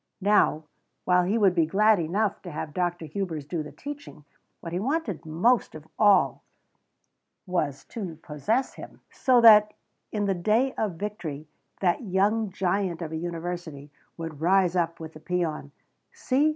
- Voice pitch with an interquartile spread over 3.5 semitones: Yes, average, 4.6 semitones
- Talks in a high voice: No, medium, 180 Hz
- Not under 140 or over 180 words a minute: Yes, average, 160 wpm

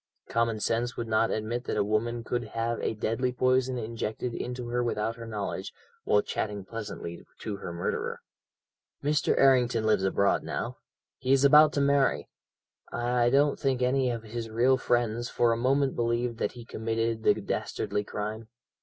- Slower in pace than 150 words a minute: No, average, 170 wpm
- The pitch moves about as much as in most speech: No, narrow, 2.3 semitones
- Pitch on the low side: Yes, low, 115 Hz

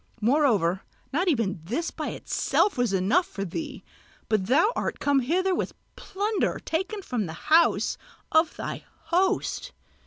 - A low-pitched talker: No, very high, 290 Hz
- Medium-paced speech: Yes, average, 145 wpm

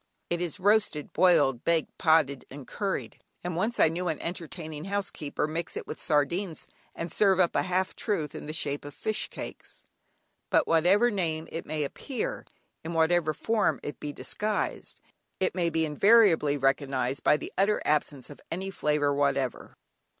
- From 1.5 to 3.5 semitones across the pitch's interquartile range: No, average, 4.1 semitones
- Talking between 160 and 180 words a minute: Yes, average, 170 wpm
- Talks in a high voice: No, medium, 160 Hz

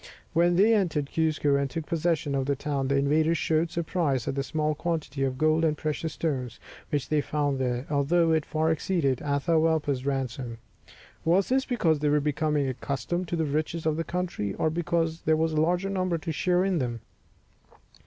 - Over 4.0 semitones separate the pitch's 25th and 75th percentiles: No, average, 3.0 semitones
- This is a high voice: No, medium, 155 Hz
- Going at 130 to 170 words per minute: No, average, 190 wpm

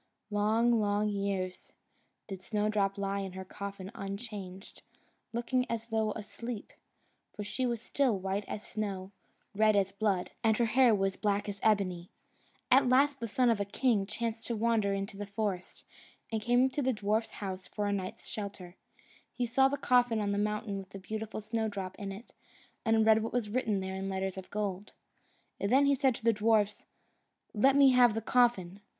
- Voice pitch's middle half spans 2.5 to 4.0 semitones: Yes, average, 2.8 semitones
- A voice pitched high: Yes, high, 210 Hz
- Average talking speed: Yes, average, 180 wpm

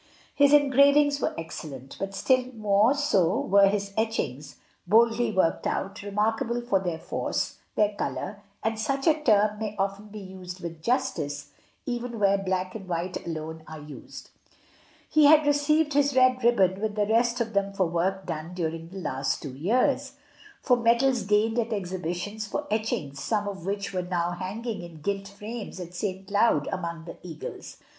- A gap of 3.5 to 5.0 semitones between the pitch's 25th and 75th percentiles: Yes, average, 4.7 semitones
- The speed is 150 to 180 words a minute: Yes, average, 175 wpm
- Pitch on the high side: Yes, high, 200 Hz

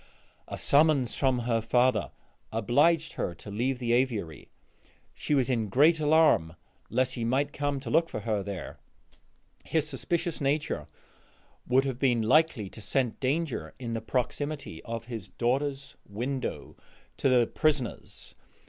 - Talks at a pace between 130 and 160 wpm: Yes, average, 145 wpm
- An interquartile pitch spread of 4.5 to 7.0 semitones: No, average, 4.0 semitones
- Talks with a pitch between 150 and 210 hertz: No, low, 130 Hz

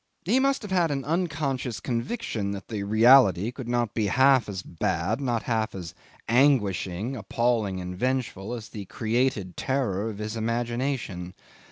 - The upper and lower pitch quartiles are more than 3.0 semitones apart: Yes, average, 4.8 semitones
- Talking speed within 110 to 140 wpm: No, average, 155 wpm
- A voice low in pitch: Yes, low, 115 Hz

